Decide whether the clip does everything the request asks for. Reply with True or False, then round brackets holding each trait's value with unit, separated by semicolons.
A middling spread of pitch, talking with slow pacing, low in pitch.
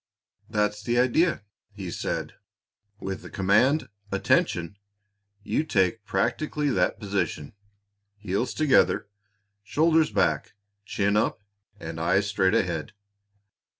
True (4.9 semitones; 105 wpm; 105 Hz)